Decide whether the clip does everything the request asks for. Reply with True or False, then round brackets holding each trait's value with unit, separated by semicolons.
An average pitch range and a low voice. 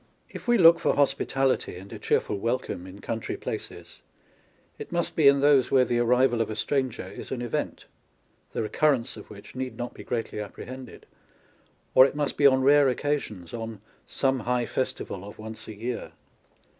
True (3.7 semitones; 125 Hz)